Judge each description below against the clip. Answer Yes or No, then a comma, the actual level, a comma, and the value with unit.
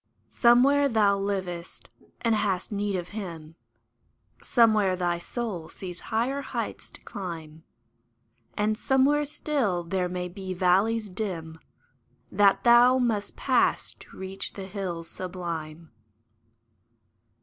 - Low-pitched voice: No, high, 195 Hz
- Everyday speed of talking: No, slow, 115 wpm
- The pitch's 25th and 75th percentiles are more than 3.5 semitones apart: Yes, average, 4.2 semitones